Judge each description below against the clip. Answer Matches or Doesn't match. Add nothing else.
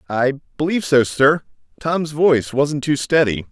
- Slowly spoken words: Doesn't match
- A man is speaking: Matches